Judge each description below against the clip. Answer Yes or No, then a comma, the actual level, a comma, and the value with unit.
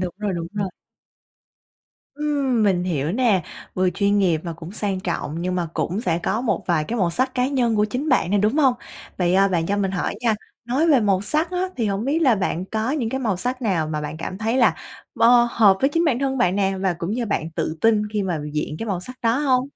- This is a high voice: Yes, high, 205 Hz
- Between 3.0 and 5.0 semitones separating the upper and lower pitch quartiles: No, wide, 5.6 semitones